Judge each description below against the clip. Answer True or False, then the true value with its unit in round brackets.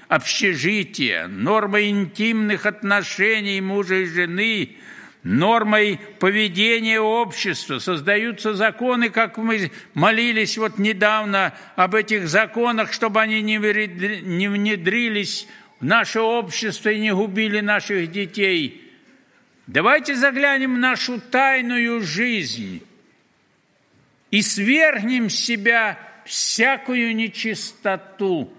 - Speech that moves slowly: True (95 wpm)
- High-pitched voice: True (215 Hz)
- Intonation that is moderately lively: False (2.3 semitones)